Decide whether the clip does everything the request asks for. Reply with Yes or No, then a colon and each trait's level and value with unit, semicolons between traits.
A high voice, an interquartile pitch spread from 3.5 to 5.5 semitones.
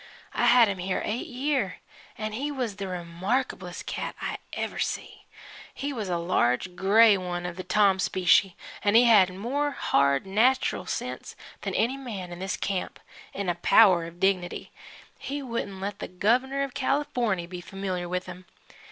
Yes: high, 195 Hz; average, 4.9 semitones